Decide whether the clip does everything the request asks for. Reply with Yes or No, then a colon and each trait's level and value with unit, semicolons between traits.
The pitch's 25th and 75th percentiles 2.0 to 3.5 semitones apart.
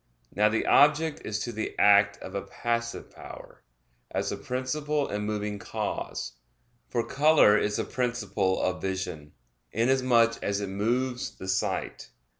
No: average, 3.9 semitones